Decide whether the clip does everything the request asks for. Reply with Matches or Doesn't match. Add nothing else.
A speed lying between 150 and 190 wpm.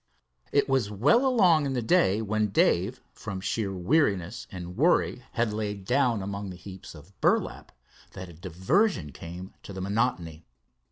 Matches